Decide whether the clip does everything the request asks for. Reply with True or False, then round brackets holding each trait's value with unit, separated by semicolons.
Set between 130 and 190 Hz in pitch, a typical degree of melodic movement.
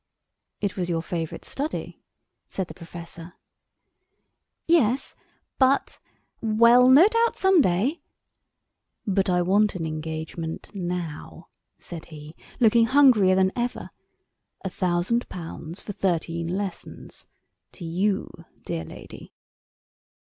False (185 Hz; 5.8 semitones)